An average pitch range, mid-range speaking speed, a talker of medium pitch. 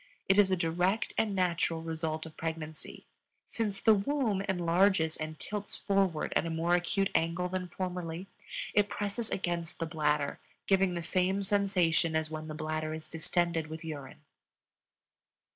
Yes: average, 3.4 semitones; average, 155 wpm; medium, 170 Hz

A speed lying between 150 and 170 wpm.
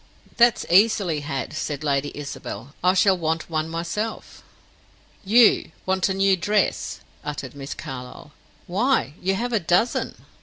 No: average, 140 wpm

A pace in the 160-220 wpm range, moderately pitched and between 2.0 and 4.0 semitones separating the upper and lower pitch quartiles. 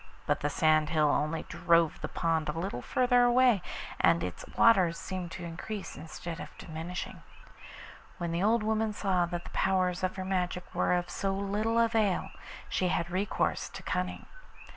Yes: average, 170 wpm; medium, 180 Hz; average, 3.5 semitones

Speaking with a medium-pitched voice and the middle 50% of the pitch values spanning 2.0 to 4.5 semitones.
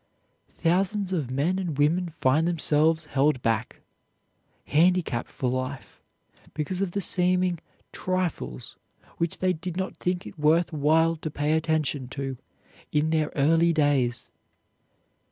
Yes: medium, 160 Hz; average, 3.5 semitones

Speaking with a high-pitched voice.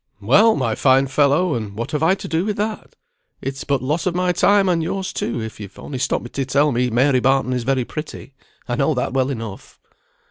No: low, 135 Hz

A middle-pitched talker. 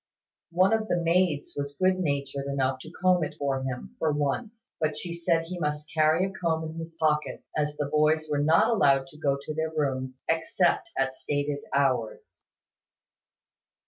Yes: medium, 155 Hz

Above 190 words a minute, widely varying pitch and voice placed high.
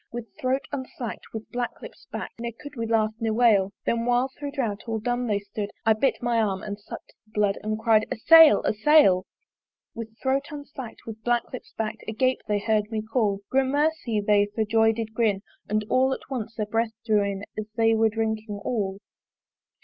No: average, 200 wpm; narrow, 2.5 semitones; high, 225 Hz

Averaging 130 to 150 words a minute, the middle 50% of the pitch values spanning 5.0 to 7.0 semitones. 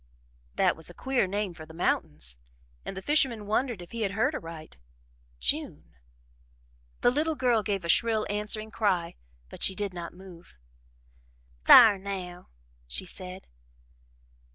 No: average, 145 wpm; average, 3.9 semitones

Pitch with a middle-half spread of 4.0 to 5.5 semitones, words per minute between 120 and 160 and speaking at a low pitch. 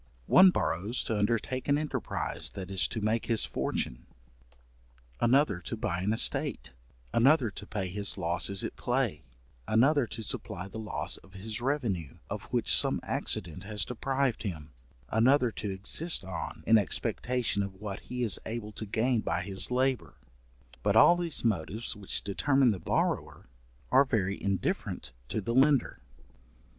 Yes: average, 4.6 semitones; average, 155 wpm; low, 110 Hz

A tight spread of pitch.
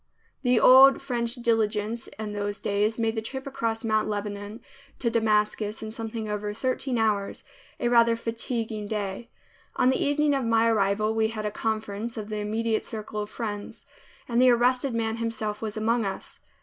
Yes: narrow, 1.9 semitones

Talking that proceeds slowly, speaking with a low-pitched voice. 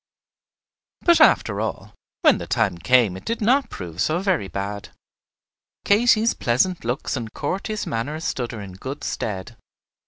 No: average, 150 wpm; low, 120 Hz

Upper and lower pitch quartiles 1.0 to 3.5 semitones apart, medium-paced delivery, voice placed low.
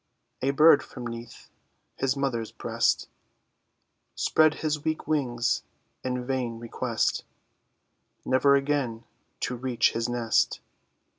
No: average, 2.9 semitones; slow, 105 wpm; low, 130 Hz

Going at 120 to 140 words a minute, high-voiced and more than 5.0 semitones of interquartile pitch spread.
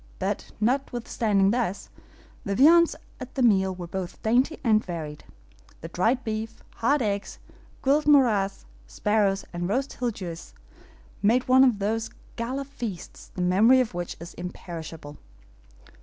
Yes: slow, 135 wpm; high, 215 Hz; wide, 5.5 semitones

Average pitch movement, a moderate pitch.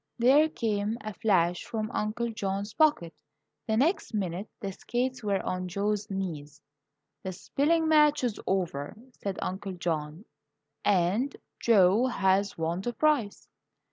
No: average, 4.5 semitones; high, 205 Hz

